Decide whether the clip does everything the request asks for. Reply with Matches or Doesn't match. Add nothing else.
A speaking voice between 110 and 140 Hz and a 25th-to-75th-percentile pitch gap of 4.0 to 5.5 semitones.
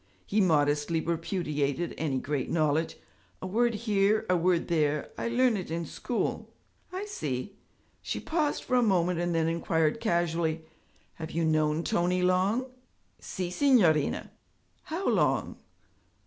Doesn't match